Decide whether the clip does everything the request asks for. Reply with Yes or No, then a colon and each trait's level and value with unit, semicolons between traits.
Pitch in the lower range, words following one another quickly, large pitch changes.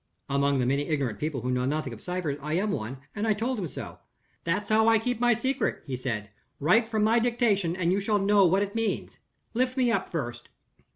No: medium, 185 Hz; fast, 225 wpm; wide, 8.1 semitones